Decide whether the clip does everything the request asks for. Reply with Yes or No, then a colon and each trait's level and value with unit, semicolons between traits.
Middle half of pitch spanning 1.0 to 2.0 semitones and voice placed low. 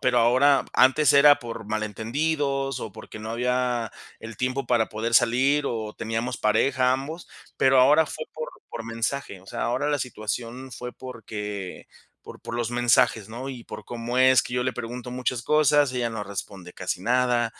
No: average, 2.7 semitones; low, 125 Hz